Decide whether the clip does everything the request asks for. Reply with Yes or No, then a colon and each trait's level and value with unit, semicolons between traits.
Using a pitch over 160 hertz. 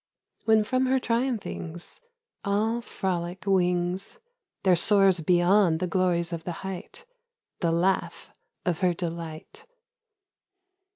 Yes: medium, 185 Hz